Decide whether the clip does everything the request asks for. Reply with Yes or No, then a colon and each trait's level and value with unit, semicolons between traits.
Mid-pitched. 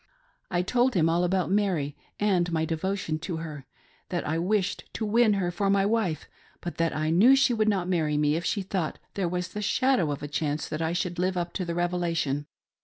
Yes: medium, 175 Hz